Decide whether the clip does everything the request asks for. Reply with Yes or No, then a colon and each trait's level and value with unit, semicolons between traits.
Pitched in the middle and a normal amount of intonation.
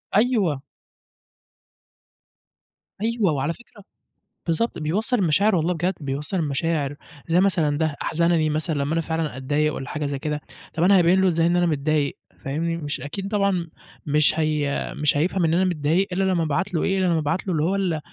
Yes: medium, 165 Hz; average, 3.6 semitones